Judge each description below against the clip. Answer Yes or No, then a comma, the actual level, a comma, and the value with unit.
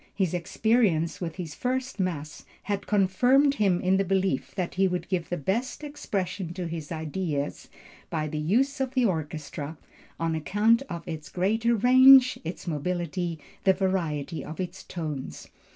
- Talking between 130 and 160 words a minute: Yes, average, 155 wpm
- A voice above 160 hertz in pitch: Yes, medium, 185 Hz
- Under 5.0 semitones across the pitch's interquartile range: Yes, average, 4.6 semitones